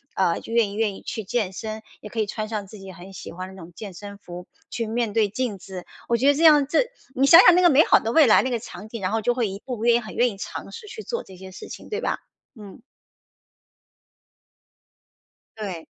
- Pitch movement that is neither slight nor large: Yes, average, 4.0 semitones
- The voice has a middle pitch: No, high, 220 Hz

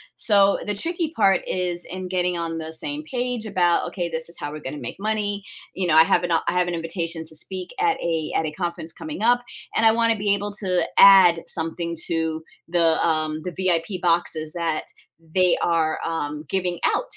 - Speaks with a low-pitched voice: No, medium, 175 Hz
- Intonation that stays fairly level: No, average, 3.5 semitones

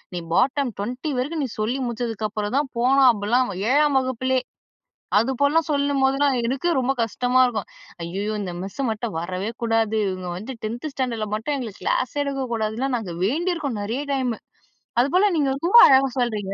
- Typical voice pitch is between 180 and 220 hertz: No, very high, 250 Hz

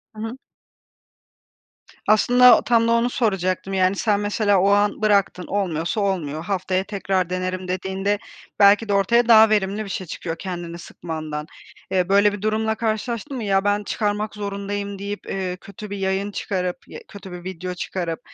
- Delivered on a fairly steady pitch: Yes, narrow, 2.3 semitones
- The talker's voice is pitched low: No, high, 200 Hz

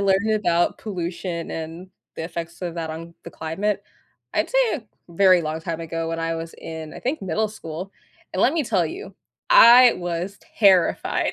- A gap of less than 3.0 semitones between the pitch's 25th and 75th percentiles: No, average, 4.0 semitones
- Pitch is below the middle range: No, medium, 175 Hz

